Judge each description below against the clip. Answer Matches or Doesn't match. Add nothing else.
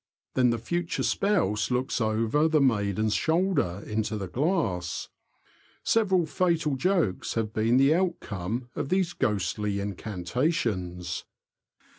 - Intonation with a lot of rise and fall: Matches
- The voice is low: Matches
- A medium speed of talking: Doesn't match